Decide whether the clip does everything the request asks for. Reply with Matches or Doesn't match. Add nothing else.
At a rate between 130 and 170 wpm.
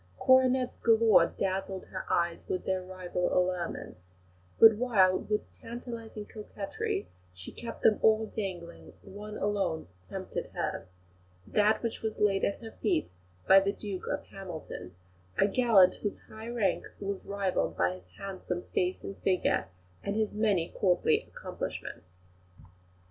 Matches